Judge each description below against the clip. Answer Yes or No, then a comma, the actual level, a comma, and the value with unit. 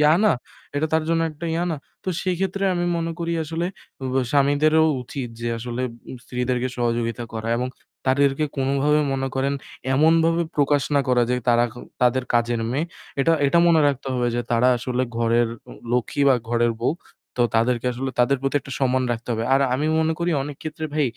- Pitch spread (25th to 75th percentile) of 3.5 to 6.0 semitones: Yes, average, 4.1 semitones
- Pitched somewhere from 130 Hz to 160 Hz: Yes, low, 135 Hz